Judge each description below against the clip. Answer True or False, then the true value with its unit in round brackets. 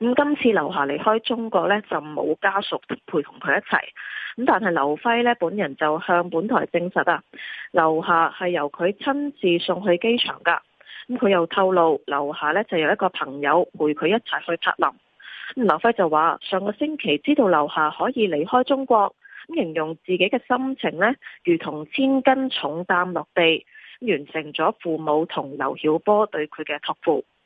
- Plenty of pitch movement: True (6.8 semitones)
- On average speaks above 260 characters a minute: False (255 characters per minute)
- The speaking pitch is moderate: True (180 Hz)